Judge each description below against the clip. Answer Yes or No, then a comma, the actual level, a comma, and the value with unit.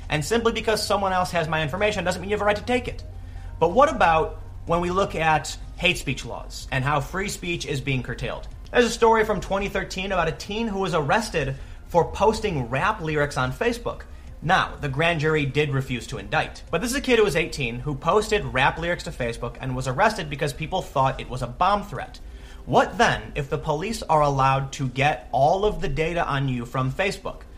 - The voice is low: No, medium, 155 Hz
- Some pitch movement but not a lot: No, wide, 6.8 semitones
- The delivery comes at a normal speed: No, fast, 220 wpm